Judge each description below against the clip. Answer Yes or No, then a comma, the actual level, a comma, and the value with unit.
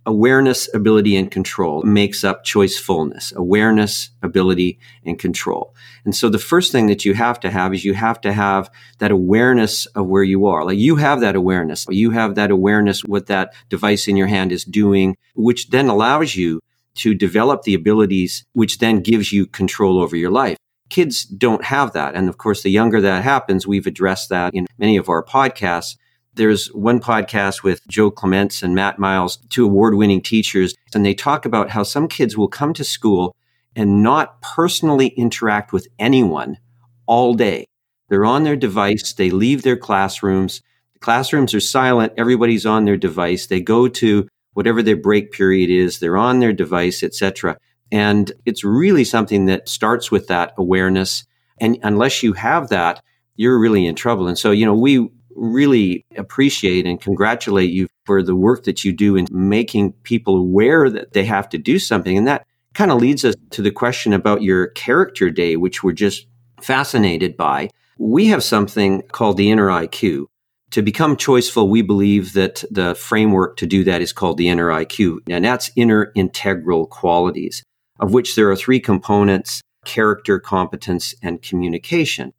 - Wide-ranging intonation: No, average, 3.8 semitones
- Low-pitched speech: Yes, low, 105 Hz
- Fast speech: No, average, 180 wpm